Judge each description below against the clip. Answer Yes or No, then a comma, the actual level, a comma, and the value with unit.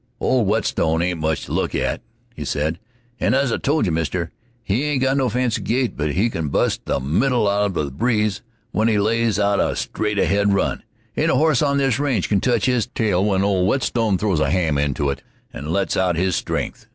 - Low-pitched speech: Yes, low, 100 Hz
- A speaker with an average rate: No, fast, 220 wpm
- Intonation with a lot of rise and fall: Yes, wide, 6.0 semitones